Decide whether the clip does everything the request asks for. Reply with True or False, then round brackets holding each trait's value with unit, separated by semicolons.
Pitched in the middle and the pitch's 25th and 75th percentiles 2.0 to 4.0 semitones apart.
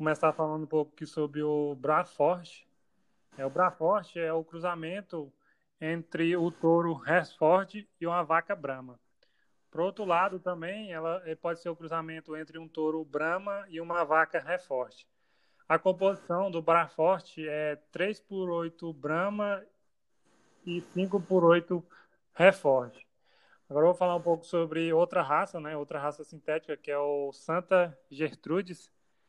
True (165 Hz; 2.5 semitones)